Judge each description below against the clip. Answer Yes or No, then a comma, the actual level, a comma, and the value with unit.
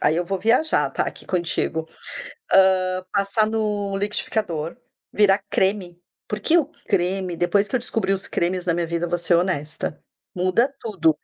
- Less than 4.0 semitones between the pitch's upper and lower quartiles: Yes, average, 3.2 semitones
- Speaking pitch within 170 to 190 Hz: Yes, medium, 185 Hz